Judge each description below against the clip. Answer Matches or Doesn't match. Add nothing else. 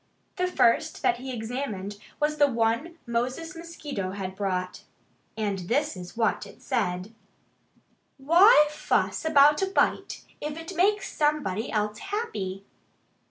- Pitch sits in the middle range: Doesn't match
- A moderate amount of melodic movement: Doesn't match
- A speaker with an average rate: Doesn't match